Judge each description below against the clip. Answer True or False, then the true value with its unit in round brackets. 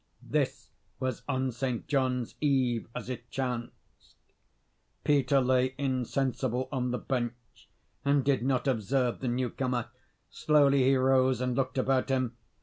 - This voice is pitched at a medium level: False (130 Hz)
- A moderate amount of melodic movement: False (1.4 semitones)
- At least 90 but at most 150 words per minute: True (135 wpm)